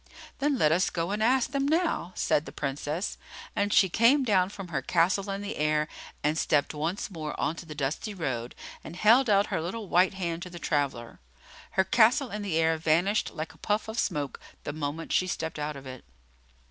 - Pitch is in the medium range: Yes, medium, 175 Hz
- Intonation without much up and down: No, average, 5.3 semitones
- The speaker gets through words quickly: Yes, fast, 210 wpm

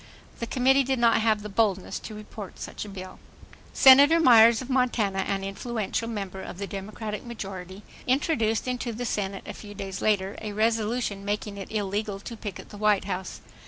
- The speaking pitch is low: No, high, 210 Hz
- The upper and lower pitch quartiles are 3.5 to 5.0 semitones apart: No, average, 2.9 semitones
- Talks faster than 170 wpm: Yes, average, 180 wpm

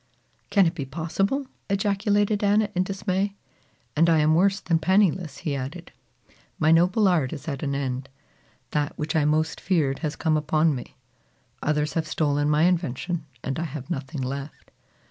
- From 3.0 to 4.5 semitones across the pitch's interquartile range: Yes, average, 4.1 semitones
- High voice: No, medium, 160 Hz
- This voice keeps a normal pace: Yes, average, 165 wpm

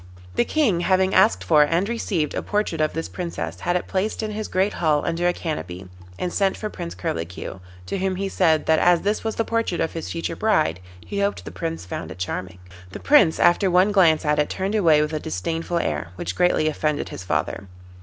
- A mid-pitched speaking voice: Yes, medium, 170 Hz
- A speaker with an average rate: No, fast, 220 wpm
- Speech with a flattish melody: No, average, 4.6 semitones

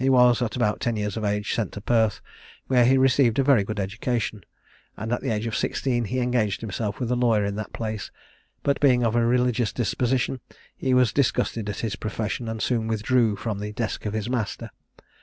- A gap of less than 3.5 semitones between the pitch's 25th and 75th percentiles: Yes, average, 2.7 semitones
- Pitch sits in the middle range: No, low, 115 Hz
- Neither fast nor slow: No, fast, 215 wpm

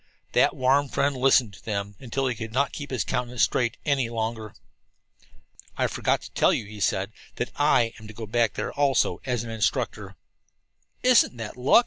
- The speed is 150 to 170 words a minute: No, average, 185 wpm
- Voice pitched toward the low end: Yes, low, 120 Hz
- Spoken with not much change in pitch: No, average, 3.3 semitones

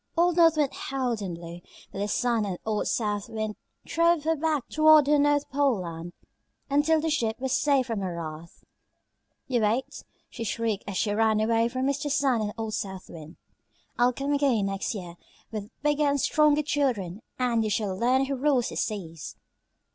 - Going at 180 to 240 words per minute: Yes, average, 185 wpm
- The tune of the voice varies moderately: No, wide, 5.7 semitones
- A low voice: No, high, 235 Hz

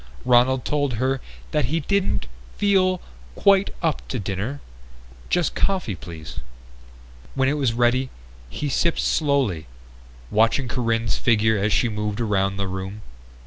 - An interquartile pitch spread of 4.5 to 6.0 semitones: Yes, wide, 5.4 semitones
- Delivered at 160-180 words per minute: No, slow, 135 wpm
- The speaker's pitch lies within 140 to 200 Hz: No, low, 120 Hz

